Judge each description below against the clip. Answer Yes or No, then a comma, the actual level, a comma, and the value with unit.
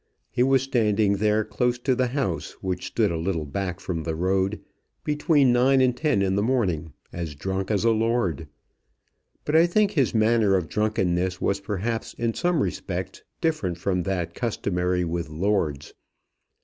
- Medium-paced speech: Yes, average, 165 wpm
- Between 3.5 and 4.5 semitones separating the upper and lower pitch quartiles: No, average, 5.3 semitones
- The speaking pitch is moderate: No, low, 100 Hz